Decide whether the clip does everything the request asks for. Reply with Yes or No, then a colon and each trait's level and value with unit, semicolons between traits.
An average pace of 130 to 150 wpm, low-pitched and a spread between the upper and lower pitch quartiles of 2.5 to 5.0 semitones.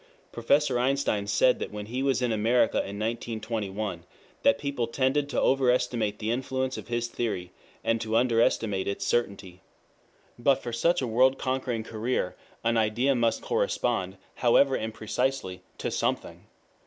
Yes: average, 145 wpm; low, 120 Hz; average, 3.3 semitones